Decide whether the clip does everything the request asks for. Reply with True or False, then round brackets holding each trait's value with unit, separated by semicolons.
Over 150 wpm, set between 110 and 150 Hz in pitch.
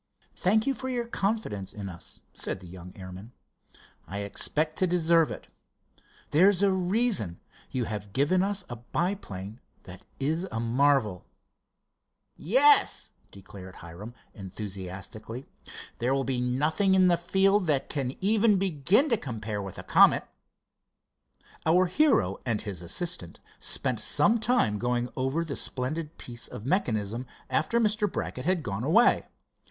False (140 wpm; 140 Hz)